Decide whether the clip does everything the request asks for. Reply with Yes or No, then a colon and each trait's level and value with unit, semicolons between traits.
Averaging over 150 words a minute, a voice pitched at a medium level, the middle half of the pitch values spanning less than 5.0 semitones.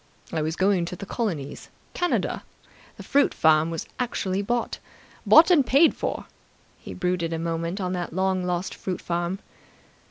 Yes: average, 160 wpm; medium, 180 Hz; average, 3.4 semitones